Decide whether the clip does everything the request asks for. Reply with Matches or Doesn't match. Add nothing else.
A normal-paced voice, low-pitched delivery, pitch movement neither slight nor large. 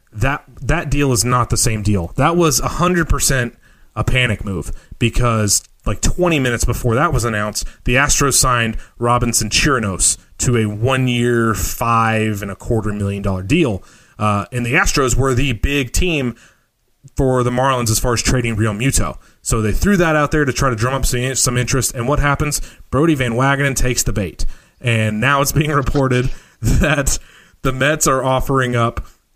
Matches